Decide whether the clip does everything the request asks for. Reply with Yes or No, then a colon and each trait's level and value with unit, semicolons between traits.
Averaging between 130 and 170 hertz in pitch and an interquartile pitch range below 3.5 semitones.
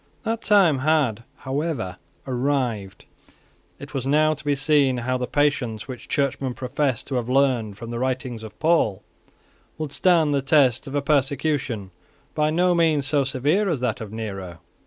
No: low, 135 Hz; average, 4.0 semitones